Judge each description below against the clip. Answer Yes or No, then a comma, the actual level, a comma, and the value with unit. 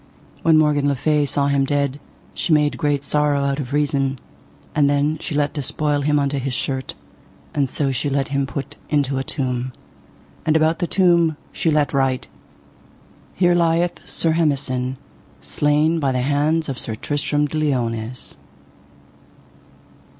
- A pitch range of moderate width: No, narrow, 2.1 semitones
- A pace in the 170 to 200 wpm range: No, average, 155 wpm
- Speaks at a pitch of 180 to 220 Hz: No, medium, 145 Hz